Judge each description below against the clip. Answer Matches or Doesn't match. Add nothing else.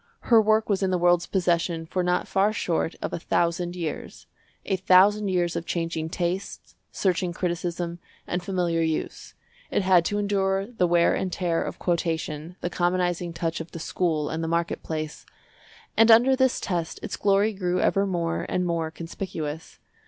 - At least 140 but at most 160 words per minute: Doesn't match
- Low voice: Doesn't match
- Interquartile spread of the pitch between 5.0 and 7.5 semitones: Doesn't match